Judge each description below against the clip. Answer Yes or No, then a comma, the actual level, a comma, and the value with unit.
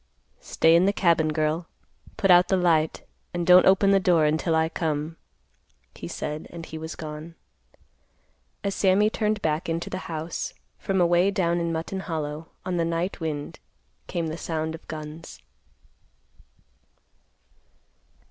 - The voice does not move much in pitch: Yes, narrow, 2.3 semitones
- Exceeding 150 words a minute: No, average, 145 wpm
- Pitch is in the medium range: Yes, medium, 165 Hz